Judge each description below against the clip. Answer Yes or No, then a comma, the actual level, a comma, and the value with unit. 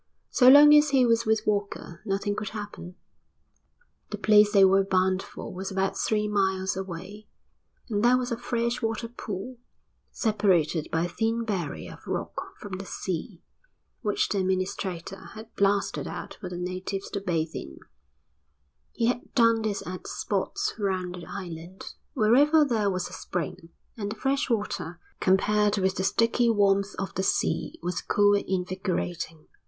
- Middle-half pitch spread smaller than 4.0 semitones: Yes, average, 3.2 semitones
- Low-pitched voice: No, high, 200 Hz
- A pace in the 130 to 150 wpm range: No, average, 160 wpm